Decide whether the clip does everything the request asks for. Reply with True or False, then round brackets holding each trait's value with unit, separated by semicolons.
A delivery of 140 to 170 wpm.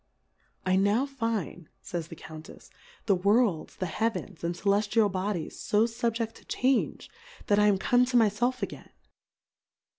True (155 wpm)